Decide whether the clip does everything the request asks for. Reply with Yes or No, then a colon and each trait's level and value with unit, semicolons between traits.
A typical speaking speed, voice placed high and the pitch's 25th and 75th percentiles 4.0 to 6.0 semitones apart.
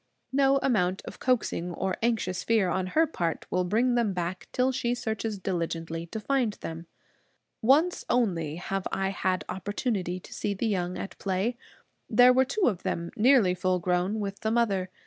Yes: average, 180 wpm; high, 195 Hz; average, 4.8 semitones